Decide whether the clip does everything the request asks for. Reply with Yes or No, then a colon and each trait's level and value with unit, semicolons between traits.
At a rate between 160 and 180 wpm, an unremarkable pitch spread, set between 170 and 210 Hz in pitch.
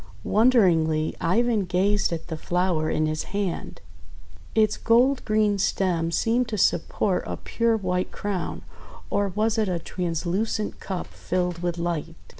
No: average, 145 wpm; average, 3.9 semitones; medium, 185 Hz